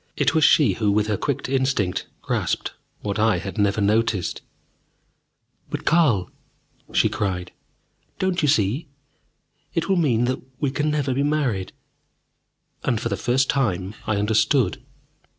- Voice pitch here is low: Yes, low, 115 Hz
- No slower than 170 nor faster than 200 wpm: No, average, 145 wpm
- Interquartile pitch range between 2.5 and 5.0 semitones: No, wide, 5.6 semitones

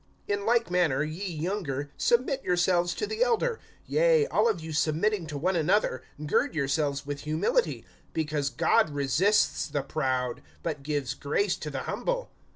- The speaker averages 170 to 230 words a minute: No, average, 160 wpm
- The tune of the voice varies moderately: No, wide, 6.3 semitones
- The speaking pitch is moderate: Yes, medium, 160 Hz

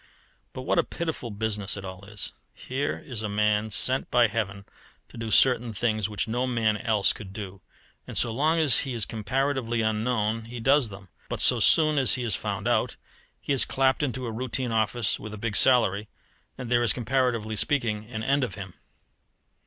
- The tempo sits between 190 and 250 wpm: Yes, average, 195 wpm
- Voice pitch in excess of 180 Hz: No, low, 115 Hz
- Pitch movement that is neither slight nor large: Yes, average, 3.2 semitones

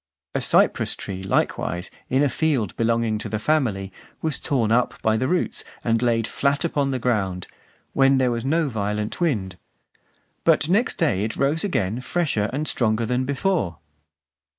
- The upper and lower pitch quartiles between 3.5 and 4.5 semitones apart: No, average, 4.9 semitones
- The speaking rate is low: No, average, 165 wpm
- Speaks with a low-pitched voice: Yes, low, 120 Hz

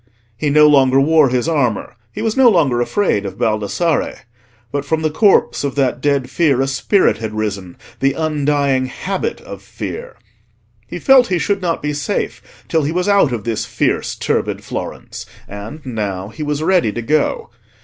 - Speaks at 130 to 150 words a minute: No, average, 175 wpm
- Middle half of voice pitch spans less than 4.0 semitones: No, average, 5.2 semitones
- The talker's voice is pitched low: No, medium, 145 Hz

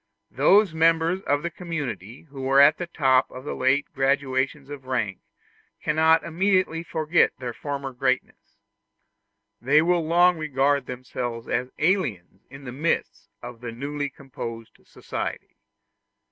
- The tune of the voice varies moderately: Yes, average, 4.0 semitones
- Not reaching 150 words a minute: Yes, slow, 135 wpm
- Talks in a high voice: No, medium, 140 Hz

